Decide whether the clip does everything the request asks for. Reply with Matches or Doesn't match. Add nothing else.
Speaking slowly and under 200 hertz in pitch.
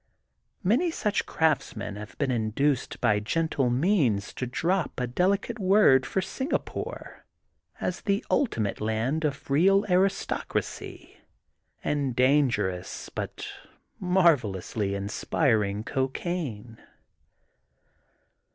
Matches